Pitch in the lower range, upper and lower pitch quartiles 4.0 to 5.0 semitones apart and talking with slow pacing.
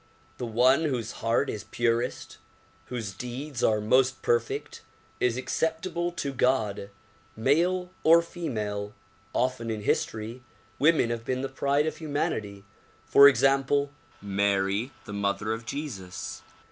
Yes: low, 125 Hz; average, 4.7 semitones; slow, 125 wpm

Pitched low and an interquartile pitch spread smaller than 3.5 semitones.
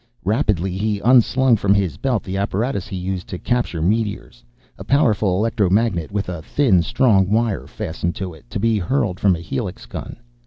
No: low, 100 Hz; average, 4.0 semitones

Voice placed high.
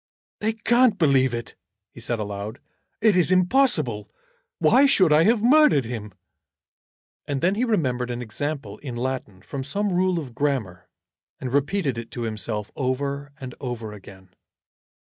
No: low, 135 Hz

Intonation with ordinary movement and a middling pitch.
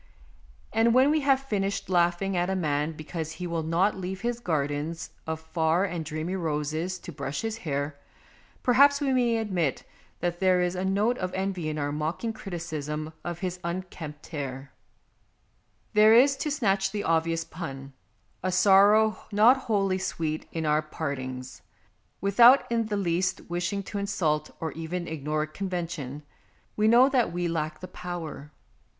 Yes: average, 4.4 semitones; medium, 175 Hz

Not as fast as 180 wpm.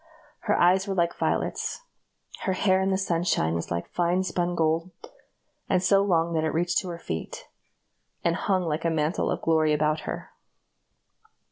Yes: average, 170 wpm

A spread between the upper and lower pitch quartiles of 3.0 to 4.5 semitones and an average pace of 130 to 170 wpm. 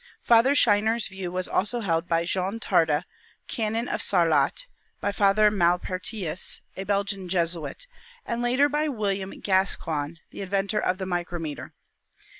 Yes: average, 3.5 semitones; average, 140 wpm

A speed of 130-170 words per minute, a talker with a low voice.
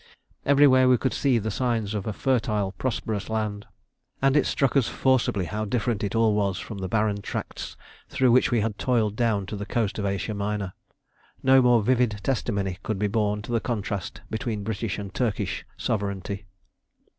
No: average, 180 wpm; low, 110 Hz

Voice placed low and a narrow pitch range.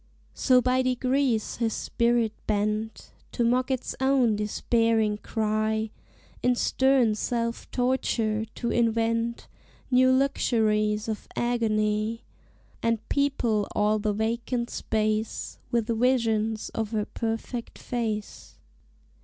No: high, 230 Hz; narrow, 2.3 semitones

